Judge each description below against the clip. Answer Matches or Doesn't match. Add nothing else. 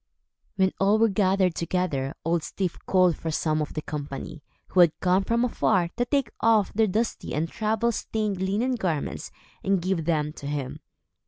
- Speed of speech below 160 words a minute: Doesn't match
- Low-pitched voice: Doesn't match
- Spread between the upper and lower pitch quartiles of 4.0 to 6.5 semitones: Matches